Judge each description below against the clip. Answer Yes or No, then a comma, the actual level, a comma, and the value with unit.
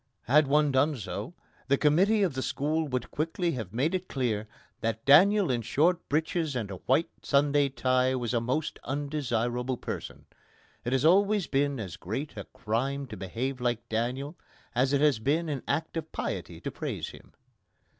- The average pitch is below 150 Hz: Yes, low, 135 Hz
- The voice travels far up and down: No, average, 4.2 semitones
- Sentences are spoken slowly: No, average, 175 wpm